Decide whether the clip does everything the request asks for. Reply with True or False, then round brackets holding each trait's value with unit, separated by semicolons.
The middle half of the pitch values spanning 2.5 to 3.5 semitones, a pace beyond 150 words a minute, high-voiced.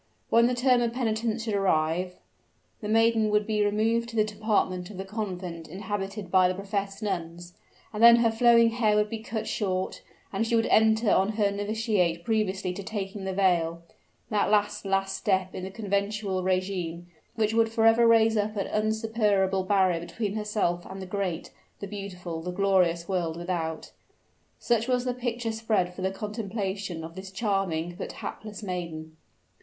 True (3.0 semitones; 170 wpm; 200 Hz)